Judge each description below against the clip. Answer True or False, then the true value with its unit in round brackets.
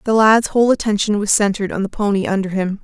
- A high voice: True (205 Hz)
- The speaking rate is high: True (235 wpm)